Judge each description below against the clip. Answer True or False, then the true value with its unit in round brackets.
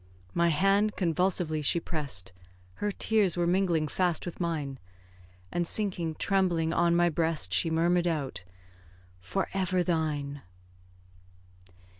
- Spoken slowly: True (120 wpm)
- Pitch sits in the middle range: True (170 Hz)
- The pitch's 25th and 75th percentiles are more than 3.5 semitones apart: False (2.9 semitones)